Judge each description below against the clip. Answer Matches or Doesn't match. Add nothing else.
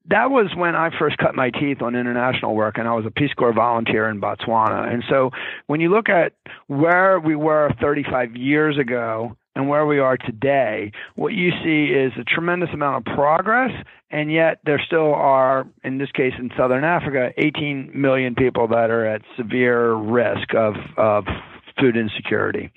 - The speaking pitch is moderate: Doesn't match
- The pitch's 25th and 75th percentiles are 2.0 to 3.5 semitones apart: Doesn't match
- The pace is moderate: Matches